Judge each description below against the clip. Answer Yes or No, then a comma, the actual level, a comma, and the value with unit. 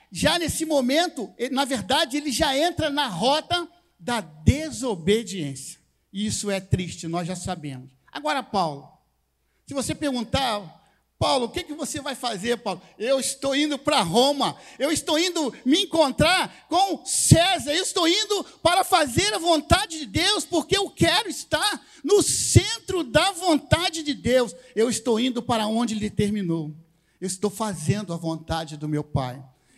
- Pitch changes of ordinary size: No, wide, 8.4 semitones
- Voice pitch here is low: No, very high, 265 Hz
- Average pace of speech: Yes, average, 160 wpm